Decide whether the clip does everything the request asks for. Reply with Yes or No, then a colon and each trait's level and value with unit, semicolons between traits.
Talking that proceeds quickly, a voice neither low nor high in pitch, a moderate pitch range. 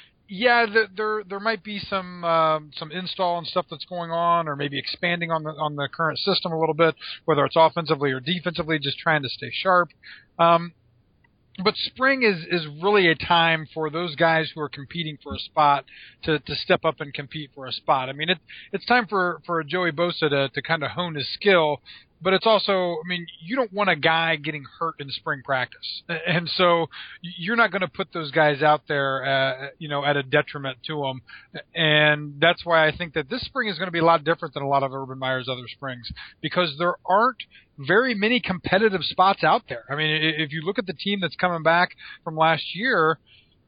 Yes: fast, 215 wpm; medium, 165 Hz; average, 3.4 semitones